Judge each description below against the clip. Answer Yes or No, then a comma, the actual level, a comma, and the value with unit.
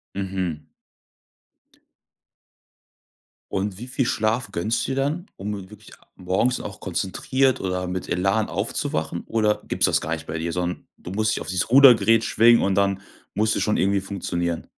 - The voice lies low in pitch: Yes, low, 100 Hz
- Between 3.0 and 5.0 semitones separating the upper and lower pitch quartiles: Yes, average, 3.6 semitones